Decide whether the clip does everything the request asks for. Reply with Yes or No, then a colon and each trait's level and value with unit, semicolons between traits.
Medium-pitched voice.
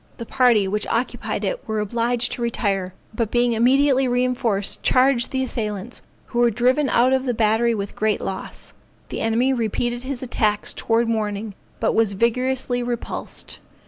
No: high, 235 Hz